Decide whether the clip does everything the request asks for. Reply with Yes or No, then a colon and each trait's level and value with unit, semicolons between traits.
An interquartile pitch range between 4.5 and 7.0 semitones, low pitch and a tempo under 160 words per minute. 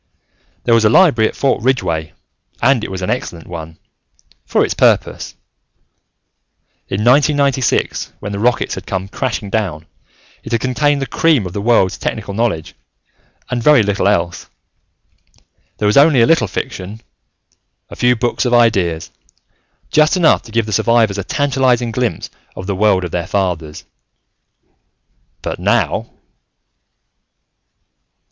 Yes: average, 4.9 semitones; low, 110 Hz; average, 140 wpm